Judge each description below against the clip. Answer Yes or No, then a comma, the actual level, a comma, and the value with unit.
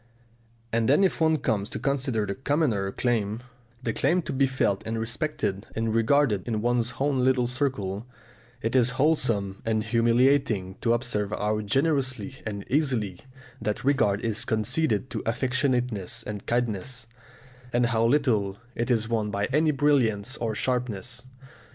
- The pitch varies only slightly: No, average, 3.8 semitones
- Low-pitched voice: Yes, low, 120 Hz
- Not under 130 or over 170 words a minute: Yes, average, 150 wpm